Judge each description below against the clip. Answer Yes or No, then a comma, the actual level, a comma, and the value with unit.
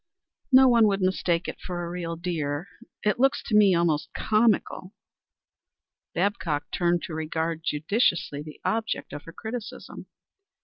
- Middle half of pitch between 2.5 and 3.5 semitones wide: No, average, 4.7 semitones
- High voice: No, medium, 175 Hz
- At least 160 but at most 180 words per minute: No, average, 140 wpm